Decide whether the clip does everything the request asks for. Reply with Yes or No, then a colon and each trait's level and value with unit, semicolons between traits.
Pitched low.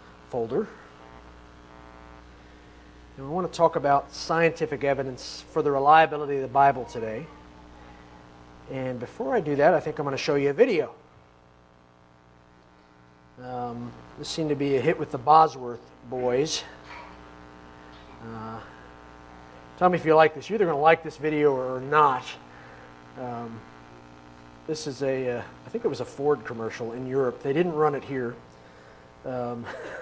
Yes: low, 115 Hz